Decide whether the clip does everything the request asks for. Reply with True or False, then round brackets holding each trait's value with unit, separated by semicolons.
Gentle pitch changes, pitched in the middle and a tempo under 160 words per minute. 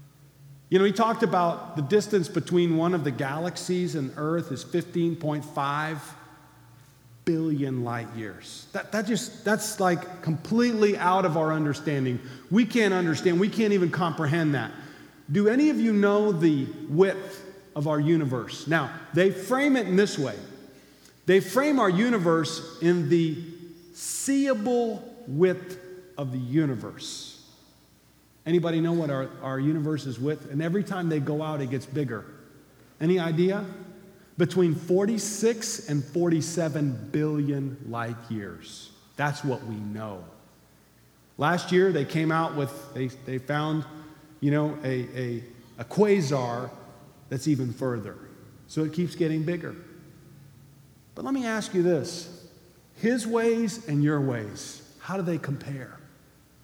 False (4.7 semitones; 160 Hz; 140 wpm)